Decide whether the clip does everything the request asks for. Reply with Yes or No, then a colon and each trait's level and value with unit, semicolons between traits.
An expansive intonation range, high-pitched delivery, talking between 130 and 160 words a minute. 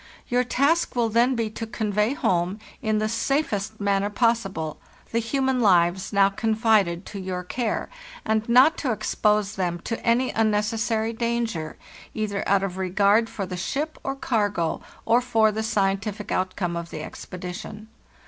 No: average, 3.1 semitones; high, 215 Hz; average, 155 wpm